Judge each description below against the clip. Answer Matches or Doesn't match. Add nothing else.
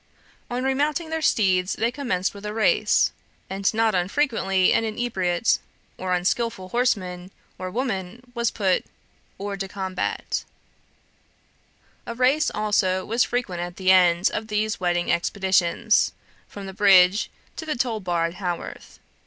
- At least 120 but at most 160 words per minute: Matches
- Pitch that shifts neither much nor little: Matches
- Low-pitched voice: Doesn't match